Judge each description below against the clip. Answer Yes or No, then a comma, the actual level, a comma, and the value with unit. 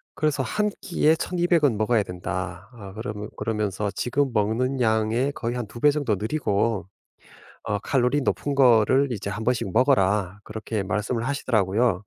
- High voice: No, low, 115 Hz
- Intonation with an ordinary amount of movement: Yes, average, 4.2 semitones